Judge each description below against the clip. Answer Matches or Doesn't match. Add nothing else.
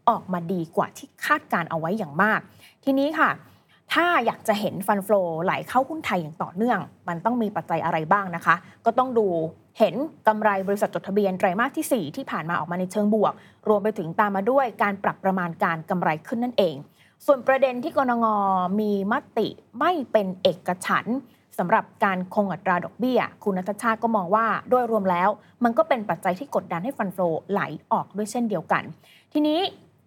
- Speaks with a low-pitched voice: Doesn't match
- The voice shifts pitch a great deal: Doesn't match